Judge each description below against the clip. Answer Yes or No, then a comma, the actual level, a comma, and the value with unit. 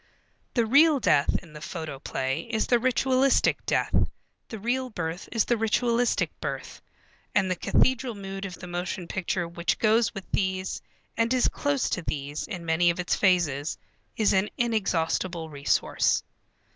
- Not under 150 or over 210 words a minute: Yes, average, 155 wpm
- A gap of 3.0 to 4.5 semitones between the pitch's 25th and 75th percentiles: No, wide, 5.6 semitones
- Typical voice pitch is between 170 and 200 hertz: Yes, high, 190 Hz